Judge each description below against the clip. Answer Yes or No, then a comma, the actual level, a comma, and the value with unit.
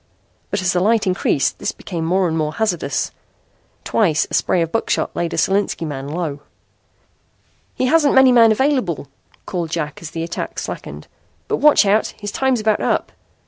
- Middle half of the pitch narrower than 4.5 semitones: No, average, 5.3 semitones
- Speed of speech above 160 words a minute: Yes, average, 175 wpm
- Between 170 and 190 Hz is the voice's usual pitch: Yes, medium, 185 Hz